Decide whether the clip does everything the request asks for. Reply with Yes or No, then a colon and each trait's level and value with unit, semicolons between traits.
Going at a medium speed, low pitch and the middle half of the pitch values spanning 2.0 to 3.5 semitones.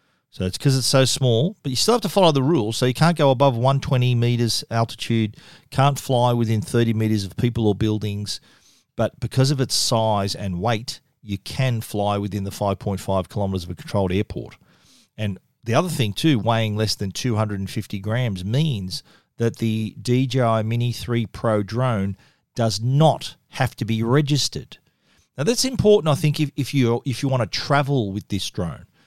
No: average, 185 wpm; low, 115 Hz; average, 4.3 semitones